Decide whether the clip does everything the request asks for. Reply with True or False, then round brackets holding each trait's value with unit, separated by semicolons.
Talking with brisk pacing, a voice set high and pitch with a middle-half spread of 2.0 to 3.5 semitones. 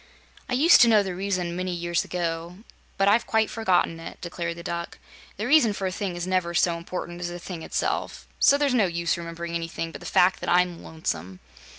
False (215 wpm; 175 Hz; 2.6 semitones)